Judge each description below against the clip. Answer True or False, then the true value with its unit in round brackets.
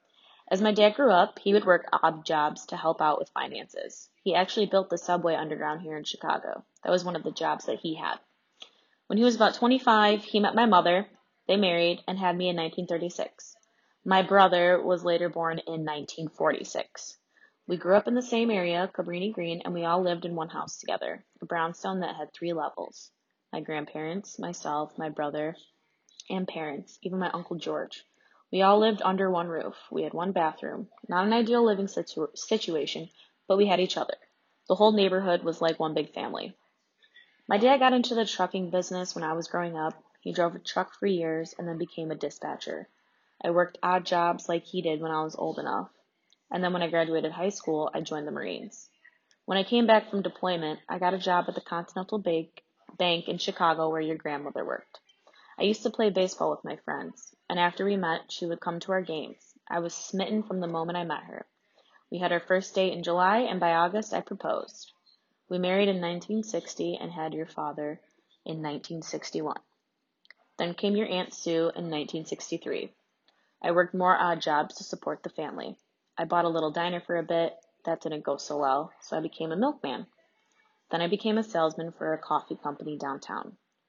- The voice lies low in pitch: False (175 Hz)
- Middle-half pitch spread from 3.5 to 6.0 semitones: False (3.1 semitones)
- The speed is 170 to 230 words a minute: True (200 wpm)